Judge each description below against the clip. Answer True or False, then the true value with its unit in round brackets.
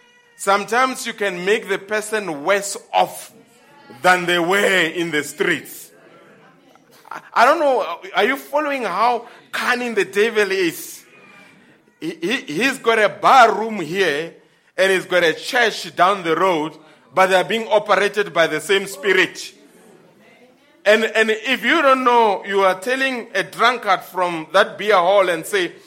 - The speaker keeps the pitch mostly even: False (4.9 semitones)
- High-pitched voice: True (215 Hz)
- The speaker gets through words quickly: False (150 wpm)